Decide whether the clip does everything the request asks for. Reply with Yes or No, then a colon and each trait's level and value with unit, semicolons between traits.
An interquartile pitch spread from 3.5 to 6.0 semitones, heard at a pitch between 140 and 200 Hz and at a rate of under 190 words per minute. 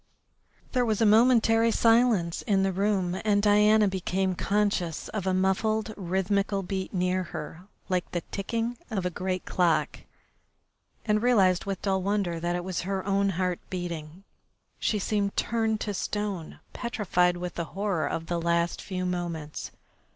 No: average, 2.9 semitones; high, 190 Hz; average, 155 wpm